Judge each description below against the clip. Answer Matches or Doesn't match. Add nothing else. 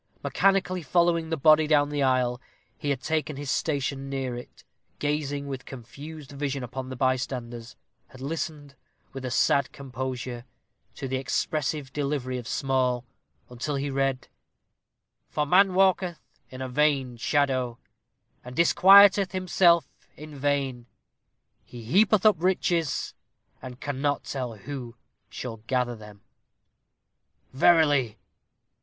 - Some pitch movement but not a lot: Matches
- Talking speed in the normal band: Doesn't match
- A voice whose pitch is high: Doesn't match